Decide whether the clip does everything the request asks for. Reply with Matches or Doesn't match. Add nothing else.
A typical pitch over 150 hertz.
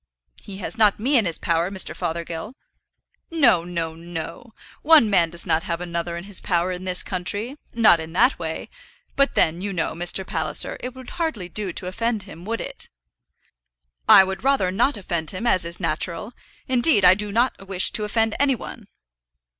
Matches